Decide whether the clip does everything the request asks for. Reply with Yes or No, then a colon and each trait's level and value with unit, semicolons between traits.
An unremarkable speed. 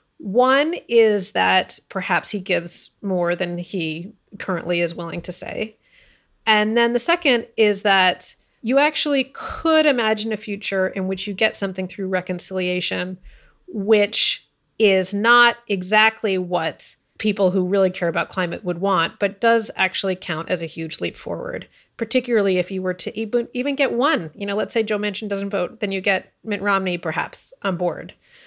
Yes: average, 165 wpm